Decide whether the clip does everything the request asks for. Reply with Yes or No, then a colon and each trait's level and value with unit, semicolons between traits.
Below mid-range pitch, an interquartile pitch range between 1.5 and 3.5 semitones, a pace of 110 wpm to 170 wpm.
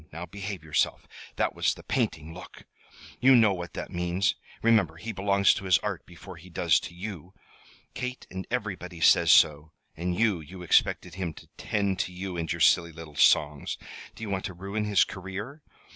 No: very low, 95 Hz; average, 2.9 semitones; average, 190 wpm